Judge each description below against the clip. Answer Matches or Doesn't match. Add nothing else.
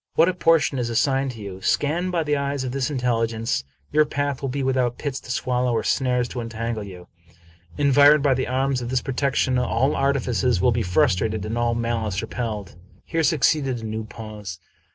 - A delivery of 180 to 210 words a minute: Matches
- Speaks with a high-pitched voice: Doesn't match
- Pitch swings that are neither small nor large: Matches